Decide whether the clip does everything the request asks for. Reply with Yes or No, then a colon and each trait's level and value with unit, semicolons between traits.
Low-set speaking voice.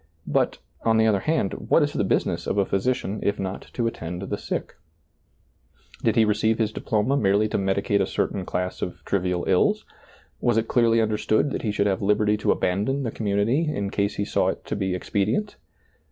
Yes: low, 105 Hz